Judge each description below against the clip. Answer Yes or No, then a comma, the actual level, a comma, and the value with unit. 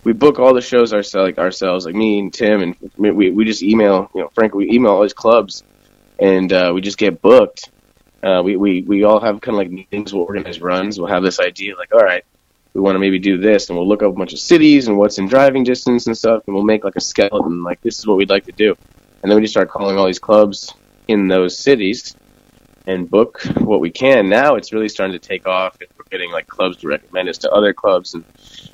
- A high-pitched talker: No, low, 100 Hz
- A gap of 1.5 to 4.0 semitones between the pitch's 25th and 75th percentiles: Yes, narrow, 2.6 semitones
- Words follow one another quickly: Yes, fast, 255 wpm